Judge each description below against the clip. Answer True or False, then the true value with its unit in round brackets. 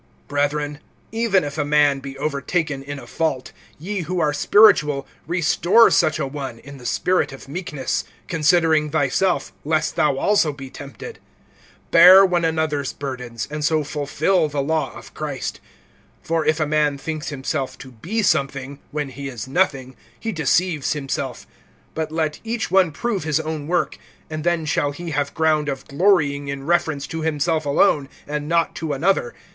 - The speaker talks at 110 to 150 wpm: False (165 wpm)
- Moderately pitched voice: True (150 Hz)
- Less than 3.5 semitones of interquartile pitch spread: True (2.9 semitones)